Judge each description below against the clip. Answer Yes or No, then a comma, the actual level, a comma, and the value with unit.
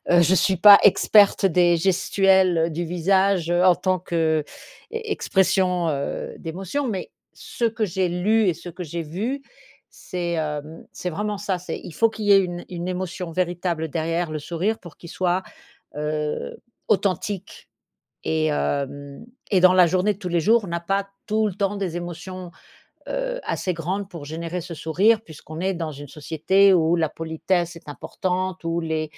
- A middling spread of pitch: Yes, average, 3.0 semitones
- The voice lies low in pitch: No, medium, 180 Hz